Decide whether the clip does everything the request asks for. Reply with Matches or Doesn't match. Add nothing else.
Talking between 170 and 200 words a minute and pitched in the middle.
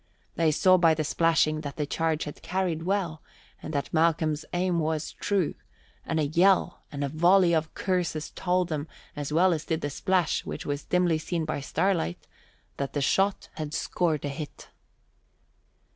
Matches